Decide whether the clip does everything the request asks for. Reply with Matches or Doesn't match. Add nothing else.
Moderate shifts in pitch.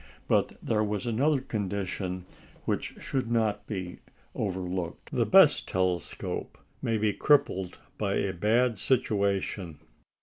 Matches